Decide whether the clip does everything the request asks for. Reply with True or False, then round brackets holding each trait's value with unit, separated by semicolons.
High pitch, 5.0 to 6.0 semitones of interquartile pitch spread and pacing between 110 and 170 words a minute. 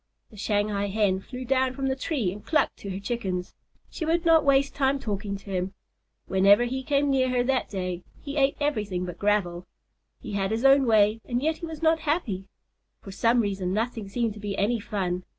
False (220 Hz; 5.4 semitones; 205 wpm)